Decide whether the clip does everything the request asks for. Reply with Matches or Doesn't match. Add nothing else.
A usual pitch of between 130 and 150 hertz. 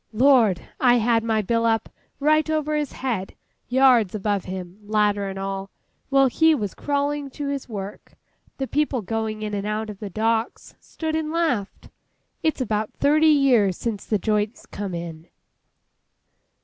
Doesn't match